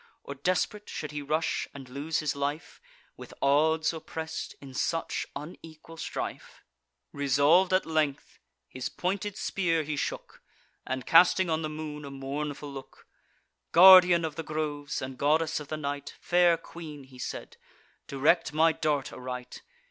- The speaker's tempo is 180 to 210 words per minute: No, average, 145 wpm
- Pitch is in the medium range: Yes, medium, 155 Hz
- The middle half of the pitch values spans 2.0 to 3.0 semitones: Yes, narrow, 2.6 semitones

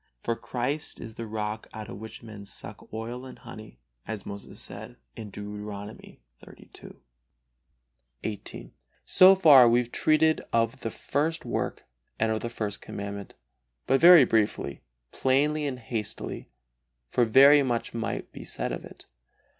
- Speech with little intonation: No, average, 4.0 semitones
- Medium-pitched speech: No, low, 115 Hz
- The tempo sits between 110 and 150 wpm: Yes, average, 145 wpm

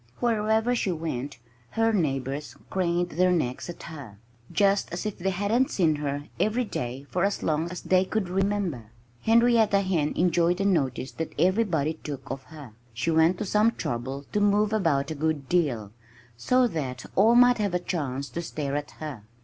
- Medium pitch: Yes, medium, 170 Hz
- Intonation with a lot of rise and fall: Yes, wide, 6.1 semitones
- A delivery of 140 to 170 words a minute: No, average, 180 wpm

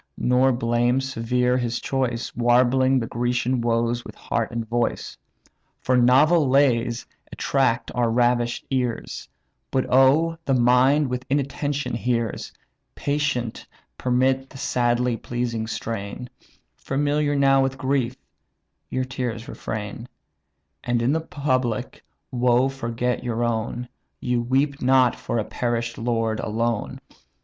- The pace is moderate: No, slow, 120 wpm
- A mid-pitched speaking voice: No, low, 125 Hz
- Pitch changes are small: Yes, narrow, 2.1 semitones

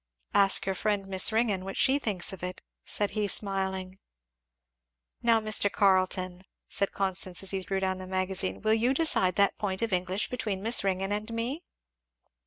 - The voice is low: No, high, 195 Hz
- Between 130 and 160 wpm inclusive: No, average, 175 wpm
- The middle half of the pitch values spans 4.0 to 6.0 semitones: No, narrow, 2.4 semitones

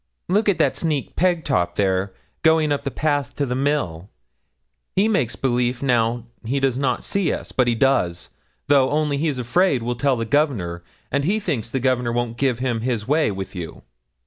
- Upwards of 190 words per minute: No, average, 185 wpm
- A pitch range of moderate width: Yes, average, 4.1 semitones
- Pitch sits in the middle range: No, low, 130 Hz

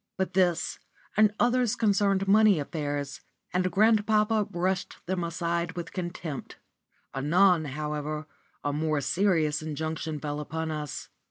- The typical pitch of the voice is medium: Yes, medium, 170 Hz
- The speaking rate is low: Yes, slow, 120 wpm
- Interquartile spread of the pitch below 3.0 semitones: No, average, 4.4 semitones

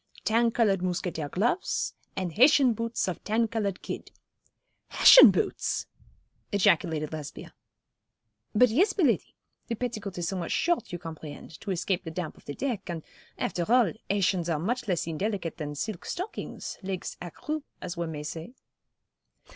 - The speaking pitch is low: No, high, 190 Hz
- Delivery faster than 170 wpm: No, average, 155 wpm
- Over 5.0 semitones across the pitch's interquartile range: Yes, wide, 5.5 semitones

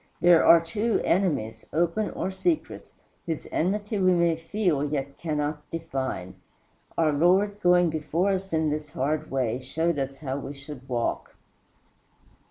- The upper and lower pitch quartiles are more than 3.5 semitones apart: Yes, average, 4.1 semitones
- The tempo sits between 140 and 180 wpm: Yes, average, 145 wpm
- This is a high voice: No, medium, 160 Hz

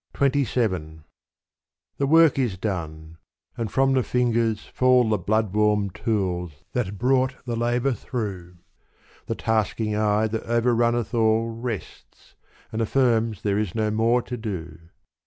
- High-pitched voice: No, low, 110 Hz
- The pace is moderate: No, slow, 130 wpm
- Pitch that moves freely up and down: No, average, 3.0 semitones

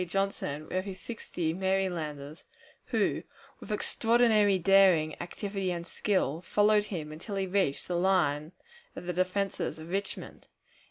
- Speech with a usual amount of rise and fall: Yes, average, 3.3 semitones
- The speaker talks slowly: Yes, slow, 130 wpm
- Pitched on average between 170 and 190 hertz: Yes, medium, 185 Hz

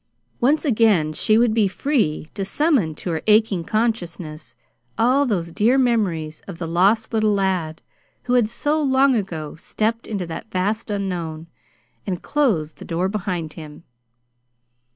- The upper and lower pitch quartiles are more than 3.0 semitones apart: Yes, wide, 5.5 semitones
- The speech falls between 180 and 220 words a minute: No, average, 150 wpm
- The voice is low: No, high, 200 Hz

